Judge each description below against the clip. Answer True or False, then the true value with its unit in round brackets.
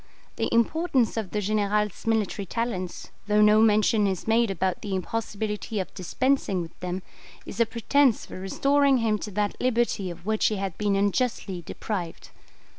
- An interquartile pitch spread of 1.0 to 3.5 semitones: True (2.9 semitones)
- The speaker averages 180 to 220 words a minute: False (165 wpm)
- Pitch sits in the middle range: False (210 Hz)